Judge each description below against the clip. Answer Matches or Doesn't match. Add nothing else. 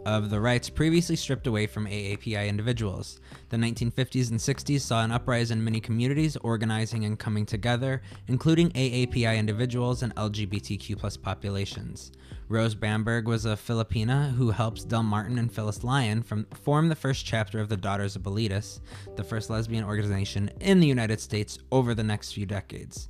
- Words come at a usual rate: Matches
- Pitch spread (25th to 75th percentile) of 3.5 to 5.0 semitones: Doesn't match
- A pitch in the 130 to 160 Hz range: Doesn't match